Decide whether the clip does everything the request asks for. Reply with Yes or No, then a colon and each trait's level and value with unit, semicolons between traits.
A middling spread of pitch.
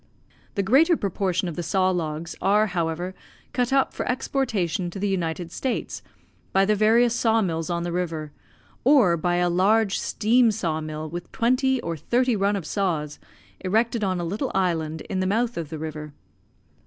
Yes: average, 4.9 semitones